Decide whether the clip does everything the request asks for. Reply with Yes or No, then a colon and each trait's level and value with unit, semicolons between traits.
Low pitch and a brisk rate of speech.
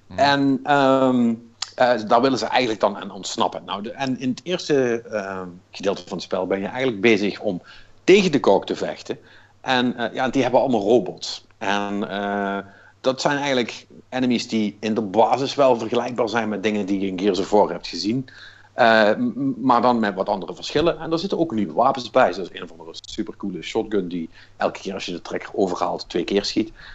Yes: low, 115 Hz; fast, 210 wpm